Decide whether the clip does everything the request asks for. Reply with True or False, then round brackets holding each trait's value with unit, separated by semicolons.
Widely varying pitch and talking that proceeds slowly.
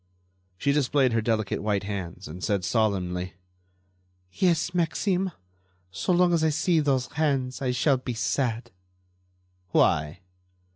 True (7.6 semitones; 130 wpm)